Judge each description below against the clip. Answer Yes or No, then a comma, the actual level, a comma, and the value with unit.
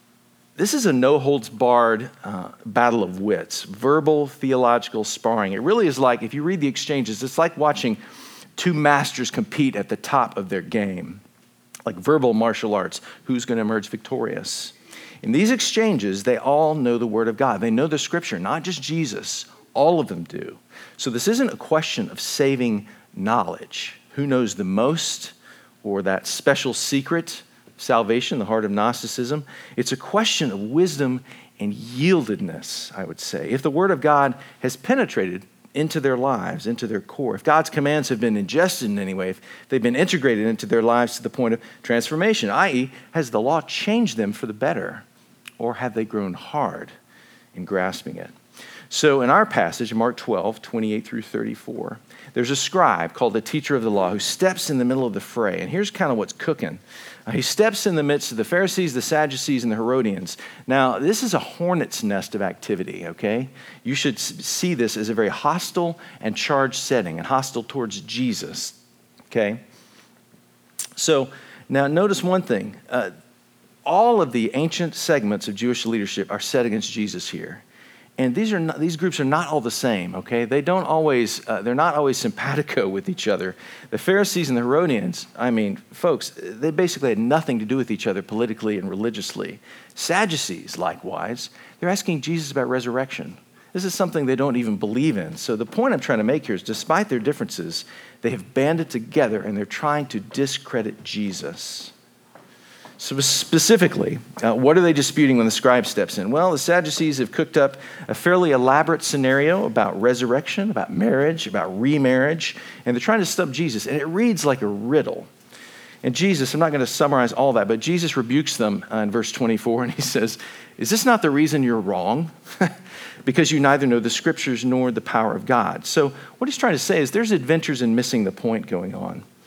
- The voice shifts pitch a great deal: Yes, wide, 6.0 semitones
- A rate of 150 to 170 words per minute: No, average, 190 wpm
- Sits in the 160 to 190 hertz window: No, low, 135 Hz